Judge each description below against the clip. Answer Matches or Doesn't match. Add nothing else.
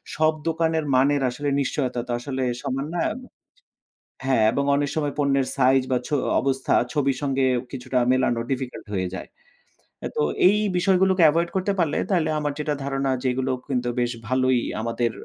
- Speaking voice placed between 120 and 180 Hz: Matches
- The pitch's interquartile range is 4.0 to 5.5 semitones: Doesn't match